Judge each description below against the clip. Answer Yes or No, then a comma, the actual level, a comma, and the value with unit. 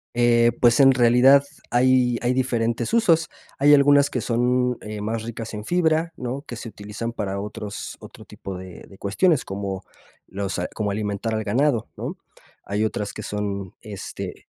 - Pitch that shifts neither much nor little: Yes, average, 3.8 semitones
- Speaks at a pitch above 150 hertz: No, low, 115 Hz